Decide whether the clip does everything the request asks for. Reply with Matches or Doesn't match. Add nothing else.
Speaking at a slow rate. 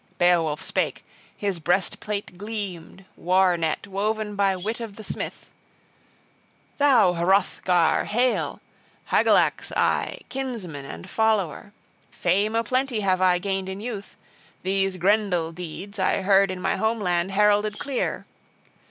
Matches